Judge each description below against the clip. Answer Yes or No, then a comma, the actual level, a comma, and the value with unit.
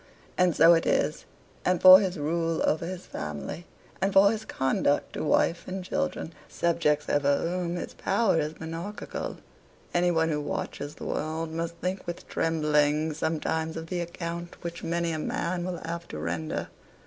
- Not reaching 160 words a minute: No, average, 170 wpm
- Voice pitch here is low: No, medium, 165 Hz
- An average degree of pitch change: No, narrow, 2.2 semitones